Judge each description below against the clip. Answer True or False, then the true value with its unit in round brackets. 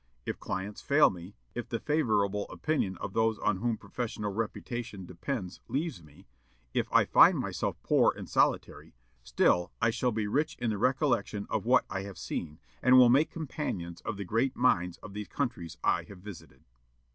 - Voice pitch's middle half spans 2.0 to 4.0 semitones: False (4.9 semitones)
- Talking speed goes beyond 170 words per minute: True (180 wpm)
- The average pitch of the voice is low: True (105 Hz)